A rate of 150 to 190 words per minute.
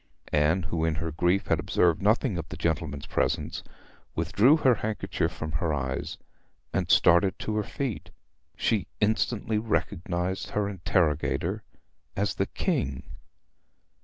No: slow, 135 wpm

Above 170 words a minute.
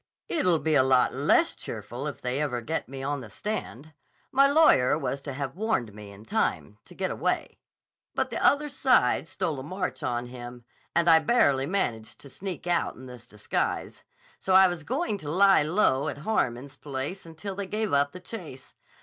Yes: average, 190 wpm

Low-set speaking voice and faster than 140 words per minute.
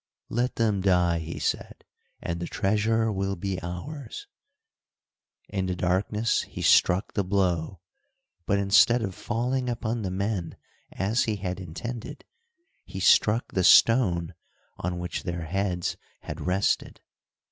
No: very low, 95 Hz; slow, 135 wpm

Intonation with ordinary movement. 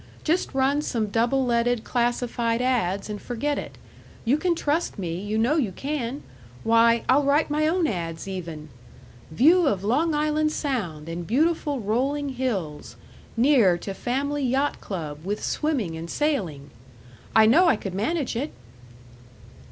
No: wide, 6.7 semitones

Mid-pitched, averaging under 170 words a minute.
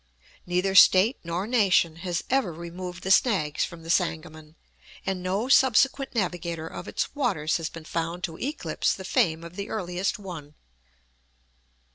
Yes: medium, 180 Hz; average, 150 wpm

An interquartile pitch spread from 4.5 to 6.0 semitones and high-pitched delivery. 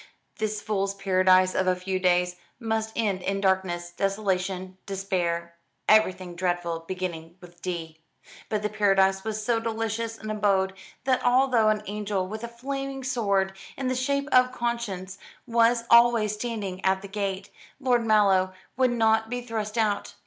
No: average, 3.5 semitones; high, 205 Hz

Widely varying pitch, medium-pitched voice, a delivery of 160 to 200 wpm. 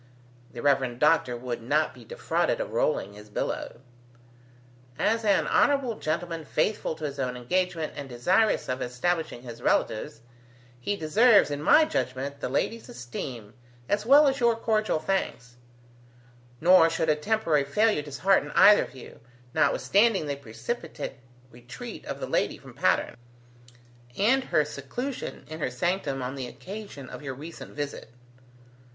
No: wide, 8.3 semitones; medium, 155 Hz; average, 145 wpm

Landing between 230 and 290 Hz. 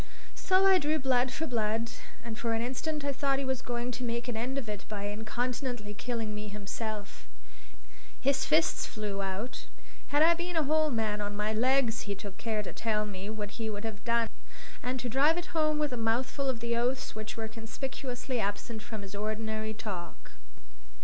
Yes: high, 235 Hz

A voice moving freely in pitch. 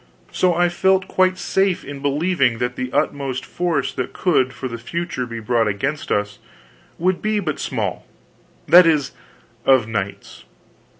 Yes: wide, 6.3 semitones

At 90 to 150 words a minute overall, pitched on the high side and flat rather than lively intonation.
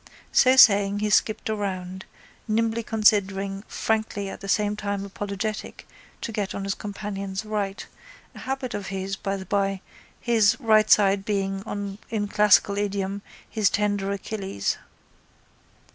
Yes: slow, 135 wpm; high, 205 Hz; narrow, 1.6 semitones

